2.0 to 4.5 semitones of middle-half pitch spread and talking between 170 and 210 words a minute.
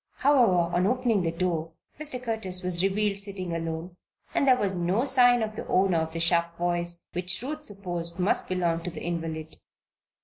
Yes: average, 4.0 semitones; average, 180 wpm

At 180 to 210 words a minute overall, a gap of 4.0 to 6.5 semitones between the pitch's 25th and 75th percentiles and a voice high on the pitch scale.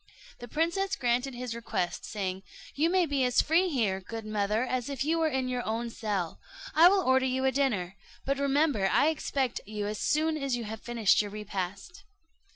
Yes: average, 195 wpm; average, 5.2 semitones; very high, 250 Hz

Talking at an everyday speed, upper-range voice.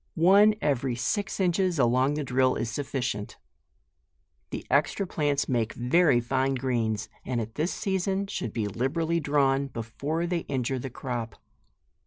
No: average, 145 wpm; low, 135 Hz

